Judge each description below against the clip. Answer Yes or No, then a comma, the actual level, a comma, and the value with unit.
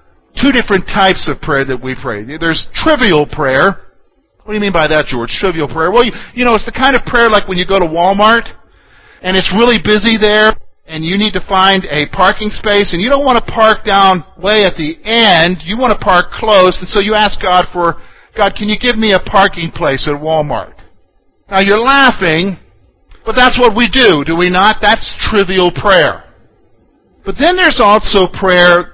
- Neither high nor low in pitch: No, high, 195 Hz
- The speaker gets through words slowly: No, fast, 205 wpm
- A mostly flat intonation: No, average, 4.1 semitones